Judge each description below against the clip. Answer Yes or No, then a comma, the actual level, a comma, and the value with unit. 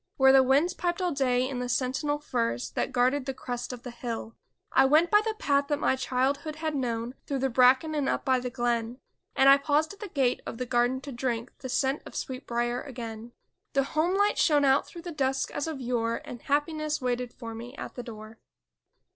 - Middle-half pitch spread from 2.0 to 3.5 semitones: Yes, average, 3.2 semitones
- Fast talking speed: Yes, fast, 220 wpm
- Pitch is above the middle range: Yes, very high, 265 Hz